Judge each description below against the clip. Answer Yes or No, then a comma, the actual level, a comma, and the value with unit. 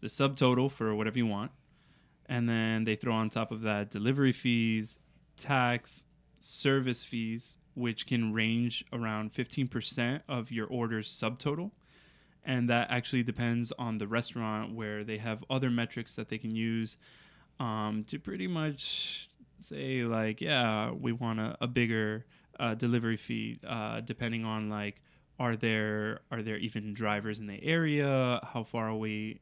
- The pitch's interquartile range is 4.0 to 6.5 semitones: No, narrow, 2.4 semitones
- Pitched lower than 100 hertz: No, low, 115 Hz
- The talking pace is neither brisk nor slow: Yes, average, 155 wpm